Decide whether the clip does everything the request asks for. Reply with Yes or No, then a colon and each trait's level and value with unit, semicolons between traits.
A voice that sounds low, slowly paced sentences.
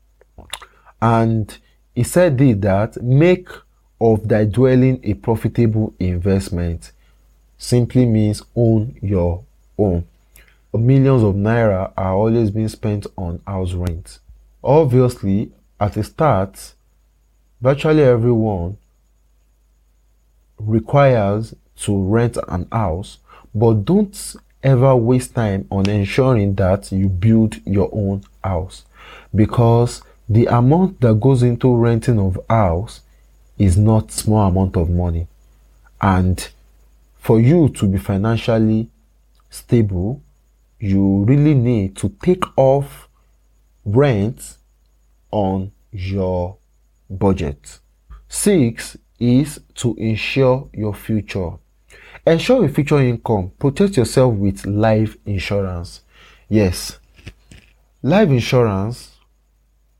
Yes: low, 105 Hz; slow, 100 wpm